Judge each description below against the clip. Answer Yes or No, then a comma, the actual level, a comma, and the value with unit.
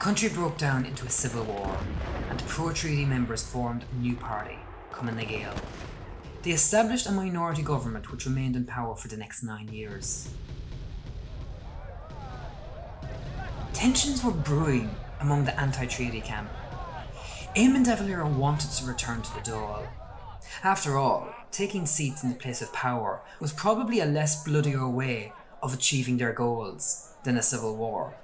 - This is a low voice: Yes, low, 130 Hz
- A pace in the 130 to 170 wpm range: Yes, average, 155 wpm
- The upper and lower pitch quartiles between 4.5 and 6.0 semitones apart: Yes, average, 5.0 semitones